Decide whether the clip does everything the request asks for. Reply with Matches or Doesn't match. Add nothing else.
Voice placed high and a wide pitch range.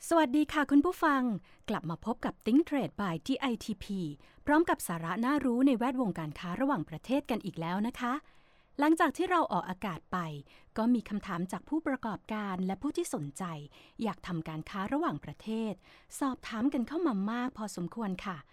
Matches